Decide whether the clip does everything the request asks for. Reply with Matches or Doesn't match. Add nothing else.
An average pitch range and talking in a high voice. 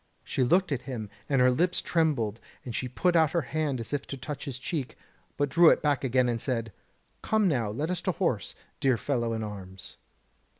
Doesn't match